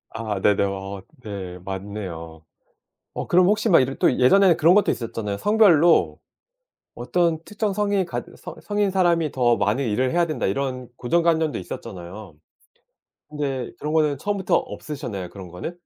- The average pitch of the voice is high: No, low, 135 Hz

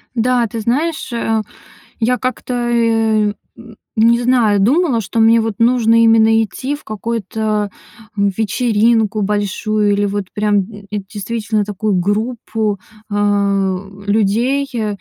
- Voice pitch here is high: Yes, high, 220 Hz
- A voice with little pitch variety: Yes, narrow, 2.2 semitones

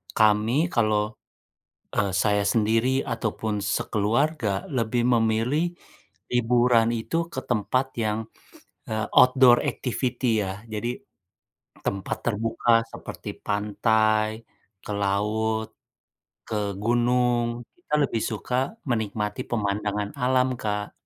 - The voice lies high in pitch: No, low, 110 Hz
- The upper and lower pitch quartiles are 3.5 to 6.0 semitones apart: No, average, 2.7 semitones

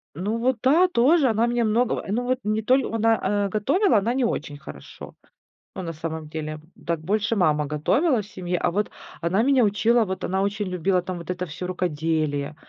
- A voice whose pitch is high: Yes, high, 200 Hz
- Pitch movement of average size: No, wide, 5.7 semitones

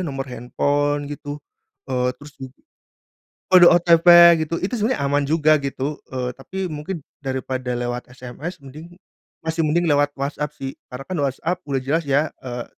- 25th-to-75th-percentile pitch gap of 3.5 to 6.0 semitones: Yes, average, 3.8 semitones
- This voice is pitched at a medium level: Yes, medium, 145 Hz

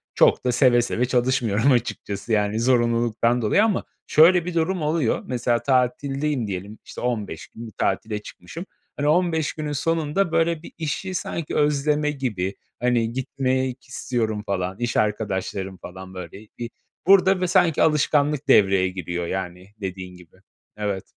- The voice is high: No, low, 125 Hz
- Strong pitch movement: Yes, wide, 6.5 semitones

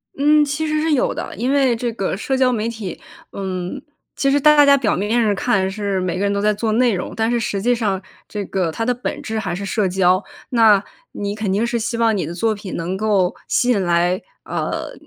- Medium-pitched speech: No, high, 215 Hz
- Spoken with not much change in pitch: No, average, 4.2 semitones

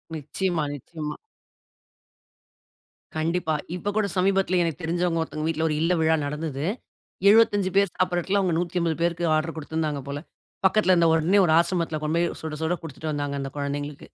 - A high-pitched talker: No, medium, 165 Hz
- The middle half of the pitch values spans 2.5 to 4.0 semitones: Yes, average, 2.8 semitones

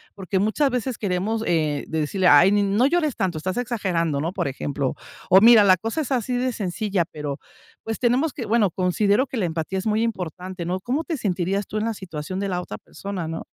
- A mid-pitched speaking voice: No, high, 195 Hz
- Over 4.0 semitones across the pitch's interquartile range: Yes, average, 4.6 semitones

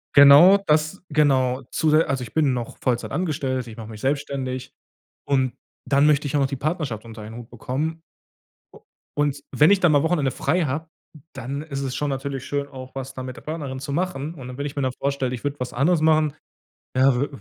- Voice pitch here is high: No, medium, 140 Hz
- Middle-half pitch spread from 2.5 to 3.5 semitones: Yes, average, 2.8 semitones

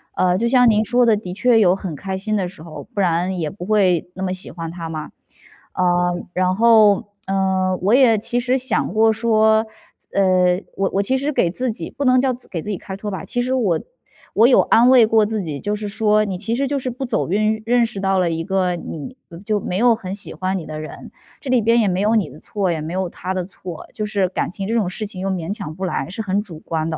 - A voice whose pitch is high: Yes, high, 200 Hz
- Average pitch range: Yes, average, 3.7 semitones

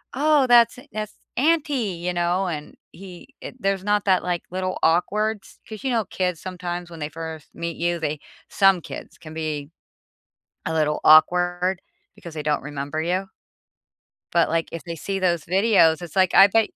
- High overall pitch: No, medium, 180 Hz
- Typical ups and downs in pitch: Yes, average, 3.4 semitones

